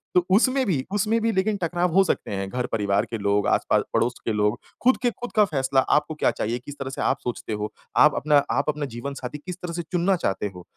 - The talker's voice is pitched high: No, medium, 145 Hz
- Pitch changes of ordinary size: No, wide, 8.0 semitones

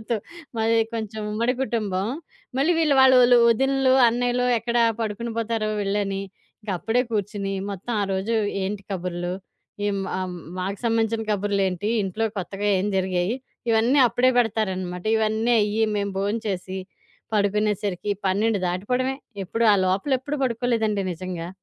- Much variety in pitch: No, average, 3.1 semitones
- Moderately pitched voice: No, high, 210 Hz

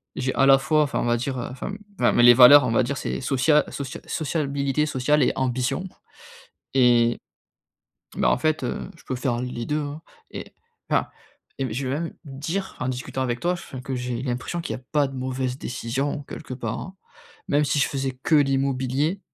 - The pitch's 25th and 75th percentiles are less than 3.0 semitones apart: Yes, narrow, 2.5 semitones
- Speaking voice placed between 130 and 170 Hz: Yes, low, 135 Hz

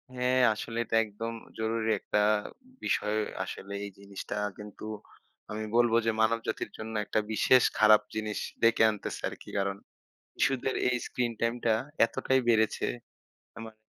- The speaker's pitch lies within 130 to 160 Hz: No, low, 110 Hz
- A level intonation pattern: Yes, narrow, 1.6 semitones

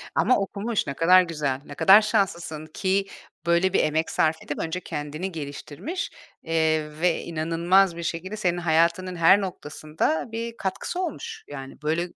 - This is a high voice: No, medium, 170 Hz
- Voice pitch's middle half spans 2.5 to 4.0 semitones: Yes, average, 3.4 semitones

